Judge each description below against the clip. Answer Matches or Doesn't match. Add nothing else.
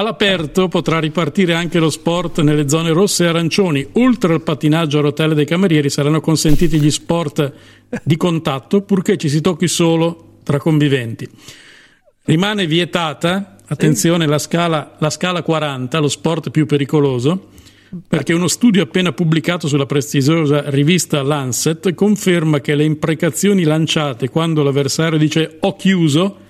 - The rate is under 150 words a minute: Matches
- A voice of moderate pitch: Matches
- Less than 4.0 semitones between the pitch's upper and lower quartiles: Matches